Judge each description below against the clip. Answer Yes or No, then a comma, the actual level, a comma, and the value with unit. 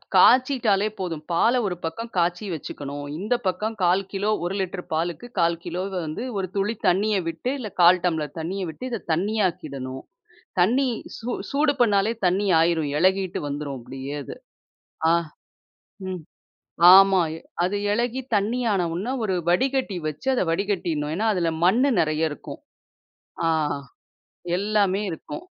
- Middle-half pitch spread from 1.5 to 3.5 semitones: No, average, 4.3 semitones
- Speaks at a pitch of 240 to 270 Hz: No, medium, 185 Hz